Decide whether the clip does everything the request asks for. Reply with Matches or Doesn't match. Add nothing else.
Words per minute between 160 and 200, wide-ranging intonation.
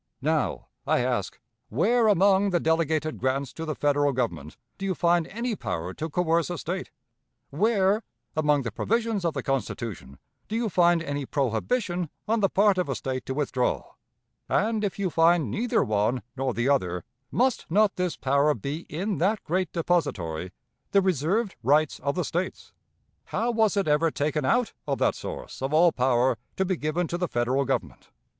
Matches